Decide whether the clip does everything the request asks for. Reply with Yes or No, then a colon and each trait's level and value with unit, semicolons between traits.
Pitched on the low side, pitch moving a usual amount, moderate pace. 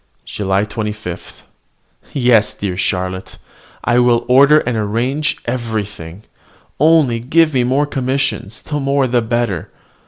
No: low, 120 Hz; average, 4.4 semitones; slow, 120 wpm